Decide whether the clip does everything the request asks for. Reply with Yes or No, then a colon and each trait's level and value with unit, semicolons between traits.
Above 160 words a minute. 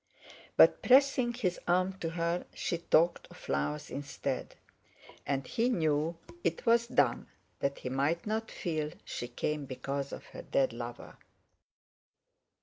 No: average, 140 wpm